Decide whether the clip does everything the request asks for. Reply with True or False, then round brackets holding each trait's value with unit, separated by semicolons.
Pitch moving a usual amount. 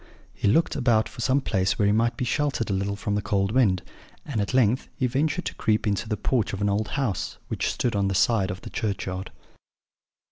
True (3.9 semitones)